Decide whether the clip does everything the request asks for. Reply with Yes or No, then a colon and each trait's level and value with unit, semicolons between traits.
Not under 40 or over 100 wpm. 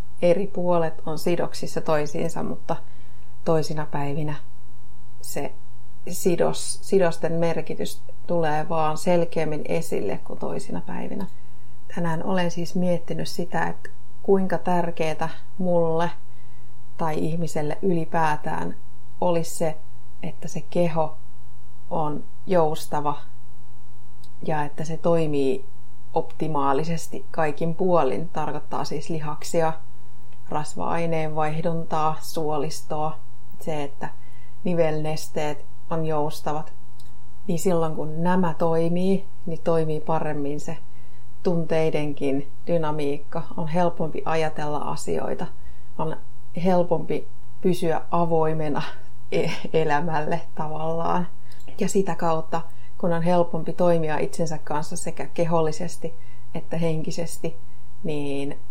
Yes: slow, 95 wpm